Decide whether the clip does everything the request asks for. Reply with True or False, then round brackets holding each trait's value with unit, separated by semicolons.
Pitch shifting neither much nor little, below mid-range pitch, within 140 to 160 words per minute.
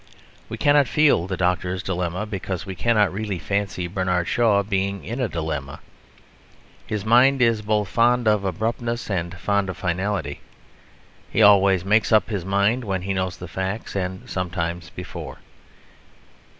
True (3.0 semitones; 100 Hz; 150 wpm)